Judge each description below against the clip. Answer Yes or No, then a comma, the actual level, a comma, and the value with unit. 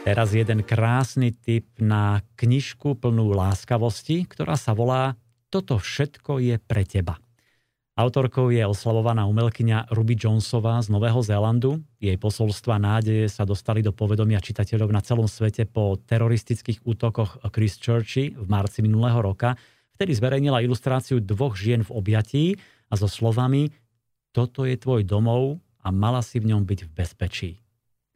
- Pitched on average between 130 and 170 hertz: No, low, 115 Hz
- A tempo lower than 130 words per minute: No, average, 145 wpm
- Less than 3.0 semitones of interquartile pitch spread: Yes, narrow, 2.5 semitones